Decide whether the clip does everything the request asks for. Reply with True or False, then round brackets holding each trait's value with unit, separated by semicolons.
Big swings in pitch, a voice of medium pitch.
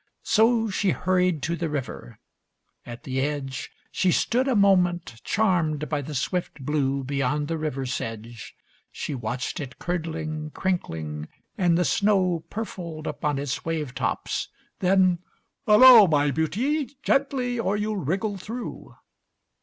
True (5.8 semitones; 165 Hz)